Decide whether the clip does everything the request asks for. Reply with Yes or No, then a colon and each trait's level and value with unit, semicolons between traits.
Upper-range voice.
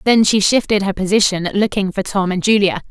Yes: high, 200 Hz